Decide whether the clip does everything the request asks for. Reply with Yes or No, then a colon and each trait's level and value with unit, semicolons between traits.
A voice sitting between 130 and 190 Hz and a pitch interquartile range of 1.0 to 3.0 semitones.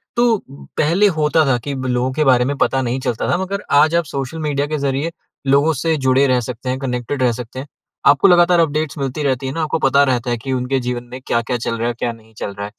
No: low, 135 Hz; average, 3.8 semitones